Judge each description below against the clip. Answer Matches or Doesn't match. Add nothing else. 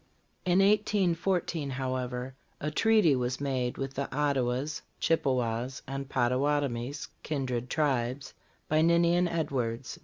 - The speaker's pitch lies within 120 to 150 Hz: Matches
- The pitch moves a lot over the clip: Doesn't match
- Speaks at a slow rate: Matches